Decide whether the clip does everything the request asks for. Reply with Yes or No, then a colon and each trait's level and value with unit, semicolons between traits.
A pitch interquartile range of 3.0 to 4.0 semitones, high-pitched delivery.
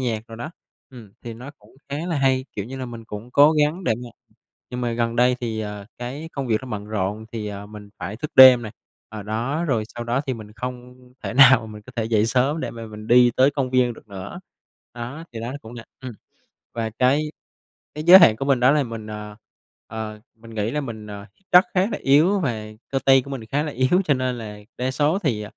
No: average, 3.6 semitones; low, 120 Hz